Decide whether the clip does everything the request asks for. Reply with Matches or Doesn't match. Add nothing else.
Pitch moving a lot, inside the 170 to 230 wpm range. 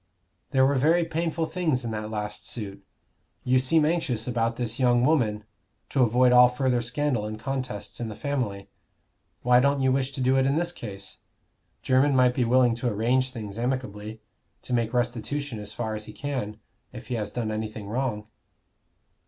Doesn't match